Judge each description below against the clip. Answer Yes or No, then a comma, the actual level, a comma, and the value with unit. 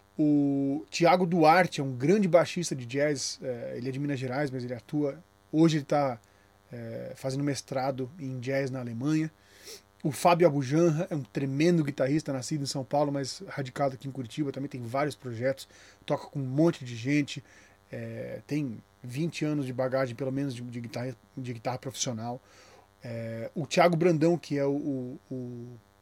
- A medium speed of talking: Yes, average, 175 wpm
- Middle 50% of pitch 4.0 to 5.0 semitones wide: No, average, 3.3 semitones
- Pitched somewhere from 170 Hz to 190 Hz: No, low, 135 Hz